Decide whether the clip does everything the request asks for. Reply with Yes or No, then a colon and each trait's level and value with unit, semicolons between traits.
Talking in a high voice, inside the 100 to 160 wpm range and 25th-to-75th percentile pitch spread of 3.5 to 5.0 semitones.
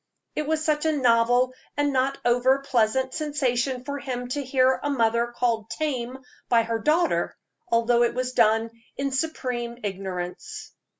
No: very high, 250 Hz; average, 155 wpm; average, 2.8 semitones